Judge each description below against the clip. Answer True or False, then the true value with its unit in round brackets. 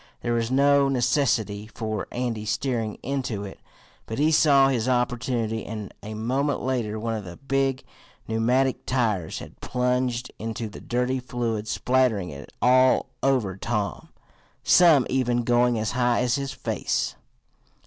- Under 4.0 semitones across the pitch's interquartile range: True (2.9 semitones)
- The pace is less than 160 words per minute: True (145 wpm)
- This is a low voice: True (120 Hz)